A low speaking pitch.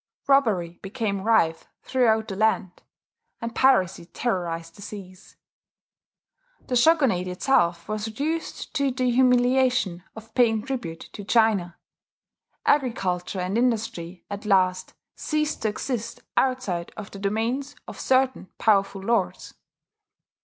No: high, 220 Hz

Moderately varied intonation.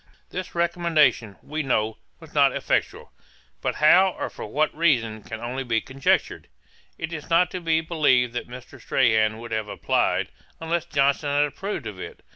No: wide, 5.7 semitones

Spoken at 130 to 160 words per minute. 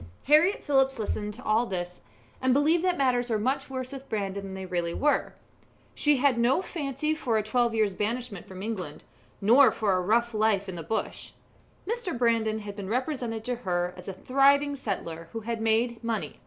No: average, 195 wpm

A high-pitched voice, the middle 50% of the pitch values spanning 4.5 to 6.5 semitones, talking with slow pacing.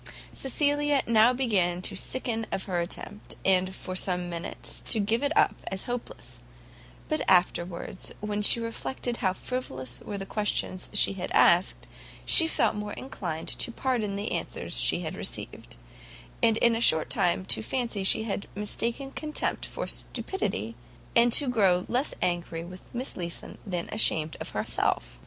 No: high, 205 Hz; average, 4.9 semitones; average, 160 wpm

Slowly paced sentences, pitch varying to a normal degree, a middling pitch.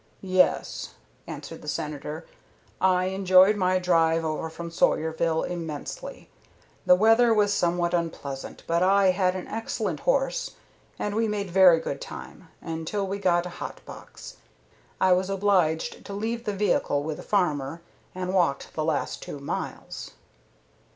No: average, 145 wpm; average, 3.6 semitones; medium, 180 Hz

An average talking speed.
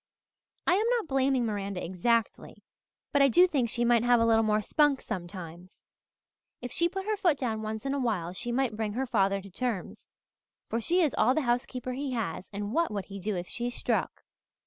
No: fast, 210 wpm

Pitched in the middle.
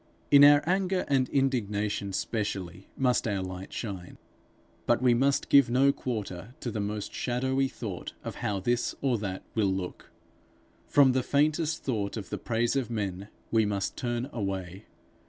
No: low, 115 Hz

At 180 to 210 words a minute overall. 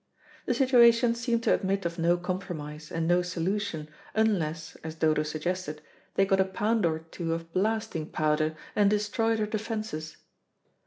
No: average, 155 wpm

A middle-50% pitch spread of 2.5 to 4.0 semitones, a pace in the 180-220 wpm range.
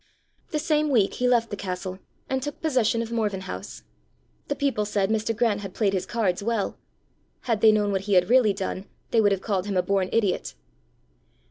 Yes: average, 3.3 semitones; fast, 205 wpm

